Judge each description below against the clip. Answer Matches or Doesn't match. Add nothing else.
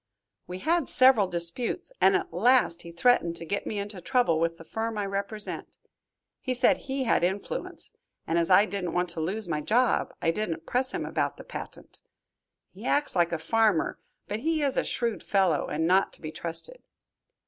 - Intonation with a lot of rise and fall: Matches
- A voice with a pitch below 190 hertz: Doesn't match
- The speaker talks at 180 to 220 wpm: Matches